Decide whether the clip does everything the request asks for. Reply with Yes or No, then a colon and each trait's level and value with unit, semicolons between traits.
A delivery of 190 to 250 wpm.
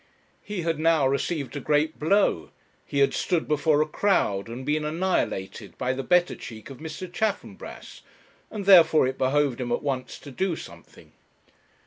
No: average, 165 wpm